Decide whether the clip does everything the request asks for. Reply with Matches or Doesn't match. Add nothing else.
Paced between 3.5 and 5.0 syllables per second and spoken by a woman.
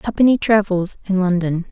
Doesn't match